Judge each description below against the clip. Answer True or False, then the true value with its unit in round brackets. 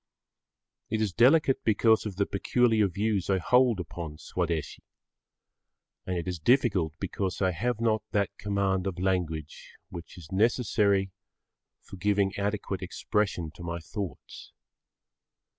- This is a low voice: True (100 Hz)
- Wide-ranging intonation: False (3.5 semitones)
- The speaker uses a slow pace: True (130 wpm)